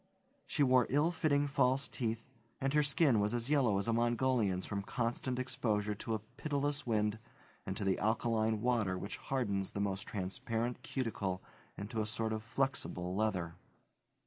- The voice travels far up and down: No, average, 4.2 semitones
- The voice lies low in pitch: Yes, low, 115 Hz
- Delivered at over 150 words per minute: Yes, average, 165 wpm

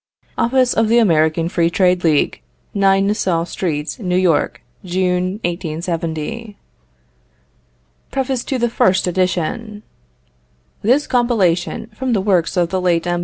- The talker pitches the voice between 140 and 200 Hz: Yes, medium, 185 Hz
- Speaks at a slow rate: Yes, slow, 120 wpm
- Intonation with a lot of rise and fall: No, average, 4.7 semitones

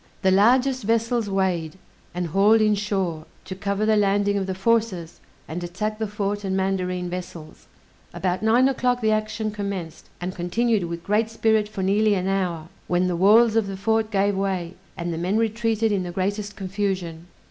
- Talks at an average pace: Yes, average, 180 wpm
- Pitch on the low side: No, high, 200 Hz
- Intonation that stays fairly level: No, average, 3.0 semitones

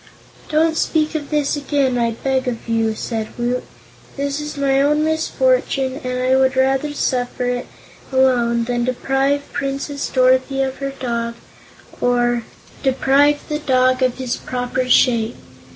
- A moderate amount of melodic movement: No, narrow, 2.3 semitones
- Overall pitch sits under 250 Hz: No, very high, 260 Hz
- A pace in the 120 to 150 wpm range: Yes, average, 145 wpm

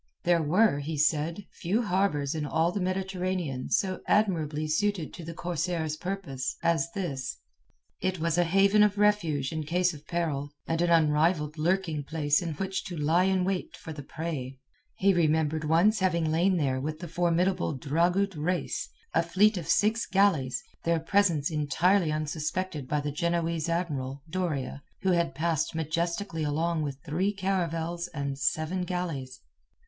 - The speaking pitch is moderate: Yes, medium, 165 Hz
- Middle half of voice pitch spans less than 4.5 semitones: Yes, average, 3.4 semitones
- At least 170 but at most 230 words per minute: No, average, 160 wpm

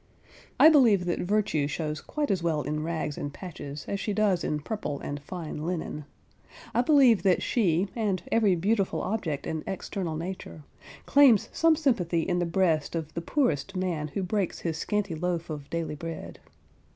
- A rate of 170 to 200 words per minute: Yes, average, 175 wpm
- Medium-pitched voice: Yes, medium, 175 Hz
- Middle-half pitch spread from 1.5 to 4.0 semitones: No, average, 4.8 semitones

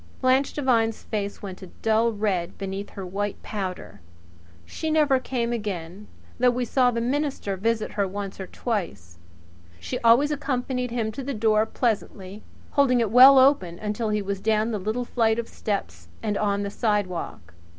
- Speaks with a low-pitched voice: No, high, 215 Hz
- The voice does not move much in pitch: No, average, 3.9 semitones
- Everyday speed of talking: Yes, average, 170 wpm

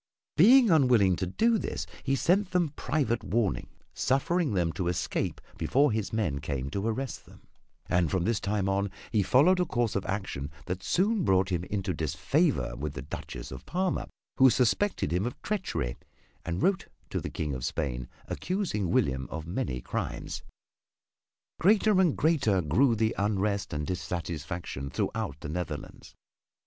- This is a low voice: Yes, low, 100 Hz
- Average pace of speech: Yes, average, 160 wpm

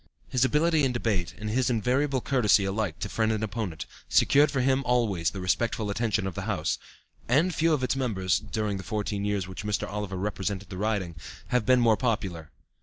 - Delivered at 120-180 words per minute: No, average, 195 wpm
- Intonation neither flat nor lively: Yes, average, 4.3 semitones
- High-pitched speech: No, low, 110 Hz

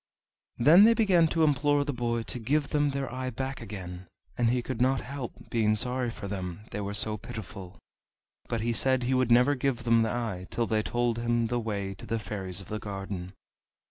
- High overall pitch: No, low, 120 Hz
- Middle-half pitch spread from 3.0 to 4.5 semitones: Yes, average, 3.7 semitones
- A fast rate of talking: Yes, fast, 210 wpm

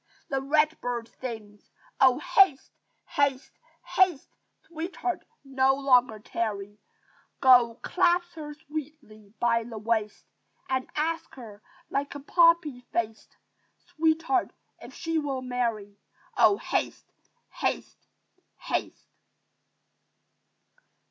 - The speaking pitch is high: Yes, very high, 270 Hz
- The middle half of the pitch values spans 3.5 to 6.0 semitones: Yes, average, 5.3 semitones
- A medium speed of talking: No, slow, 100 wpm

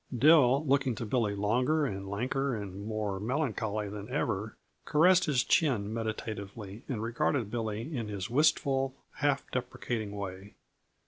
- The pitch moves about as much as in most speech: Yes, average, 4.7 semitones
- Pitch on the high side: No, low, 115 Hz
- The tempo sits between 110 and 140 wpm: Yes, slow, 135 wpm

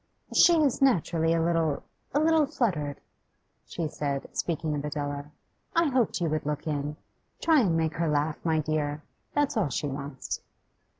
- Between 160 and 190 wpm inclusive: Yes, average, 165 wpm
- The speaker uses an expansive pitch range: Yes, wide, 6.7 semitones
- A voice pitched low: No, medium, 160 Hz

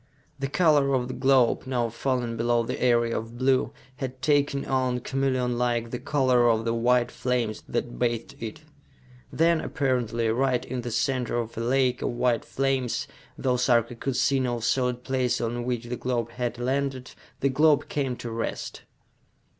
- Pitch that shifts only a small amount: Yes, narrow, 1.9 semitones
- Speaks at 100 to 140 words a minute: No, average, 170 wpm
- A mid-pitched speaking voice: No, low, 125 Hz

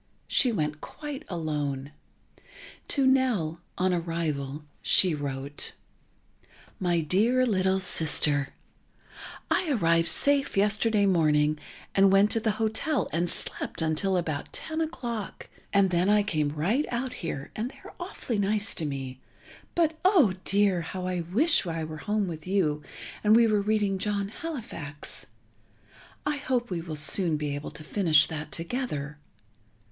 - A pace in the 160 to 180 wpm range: No, average, 145 wpm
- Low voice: No, medium, 185 Hz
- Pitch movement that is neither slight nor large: No, wide, 6.2 semitones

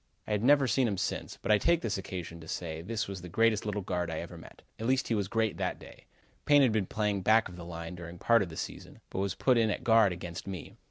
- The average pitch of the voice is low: Yes, low, 100 Hz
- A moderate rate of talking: No, fast, 275 wpm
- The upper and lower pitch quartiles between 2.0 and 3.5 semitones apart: No, average, 4.4 semitones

